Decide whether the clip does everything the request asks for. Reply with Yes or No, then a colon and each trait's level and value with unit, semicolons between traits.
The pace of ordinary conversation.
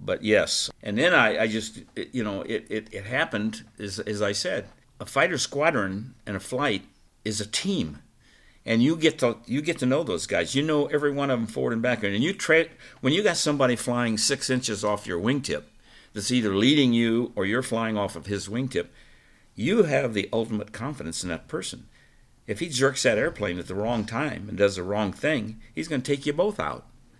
No: fast, 220 wpm